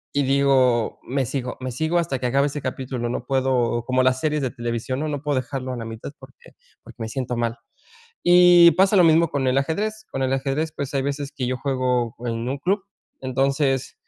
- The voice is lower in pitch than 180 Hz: Yes, low, 135 Hz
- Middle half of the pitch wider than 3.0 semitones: No, narrow, 2.5 semitones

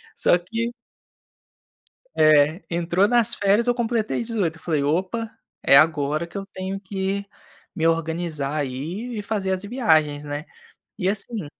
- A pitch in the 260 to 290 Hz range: No, medium, 185 Hz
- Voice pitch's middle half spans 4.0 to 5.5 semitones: Yes, average, 5.2 semitones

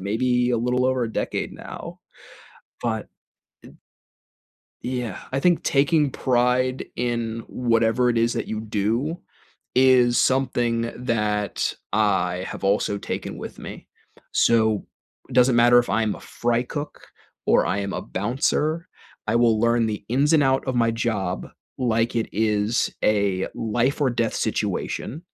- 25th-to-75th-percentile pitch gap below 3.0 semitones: Yes, narrow, 2.5 semitones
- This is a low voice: Yes, low, 120 Hz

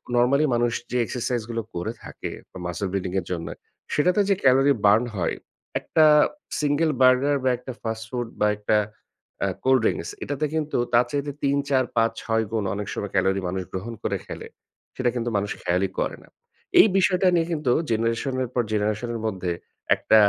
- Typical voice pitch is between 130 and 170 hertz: No, low, 120 Hz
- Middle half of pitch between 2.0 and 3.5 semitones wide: No, average, 4.8 semitones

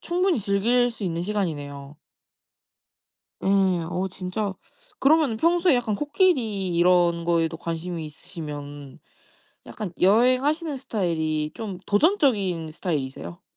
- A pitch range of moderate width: No, wide, 6.8 semitones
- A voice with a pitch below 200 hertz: Yes, high, 190 Hz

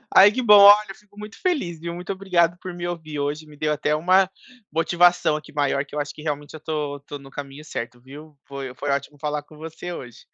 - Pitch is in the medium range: Yes, medium, 155 Hz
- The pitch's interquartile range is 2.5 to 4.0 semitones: Yes, average, 3.4 semitones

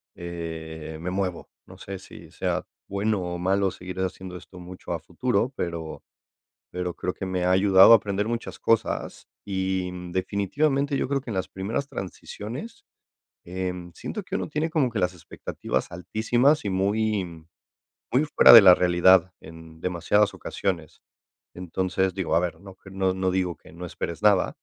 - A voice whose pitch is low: Yes, very low, 95 Hz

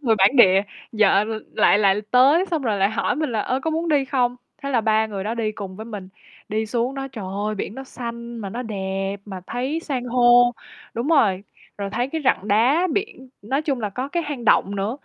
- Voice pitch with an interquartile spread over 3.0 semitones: Yes, average, 4.5 semitones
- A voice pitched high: Yes, high, 235 Hz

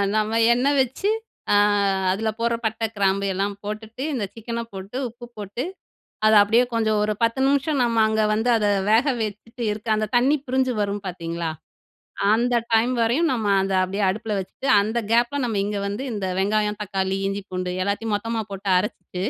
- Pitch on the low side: No, high, 215 Hz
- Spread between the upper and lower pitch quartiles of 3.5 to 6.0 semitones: No, average, 2.8 semitones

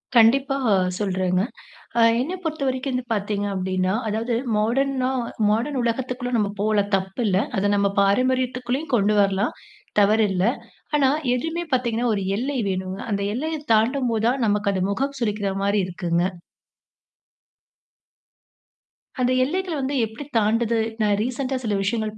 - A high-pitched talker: Yes, high, 225 Hz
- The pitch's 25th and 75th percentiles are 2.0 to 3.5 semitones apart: No, average, 4.3 semitones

